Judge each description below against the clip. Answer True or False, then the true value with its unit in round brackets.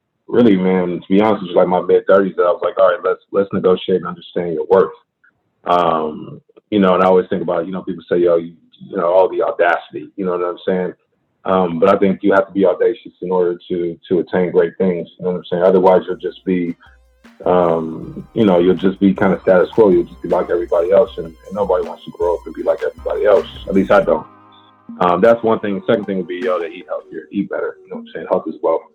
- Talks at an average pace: False (265 wpm)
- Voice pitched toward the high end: False (100 Hz)